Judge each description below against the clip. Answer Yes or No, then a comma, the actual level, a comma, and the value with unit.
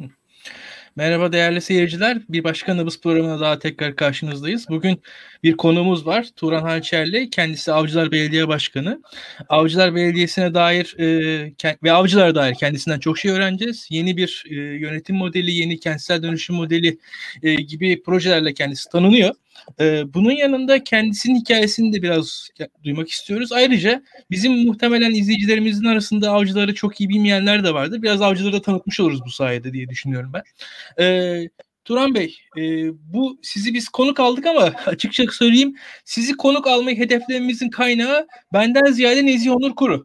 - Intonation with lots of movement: Yes, wide, 6.4 semitones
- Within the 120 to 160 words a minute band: Yes, fast, 140 wpm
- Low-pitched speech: No, medium, 185 Hz